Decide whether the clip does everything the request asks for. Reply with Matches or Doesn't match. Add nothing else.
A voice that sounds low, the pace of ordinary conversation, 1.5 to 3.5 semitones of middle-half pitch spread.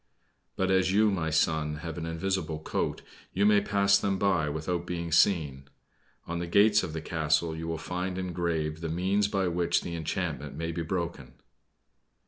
Matches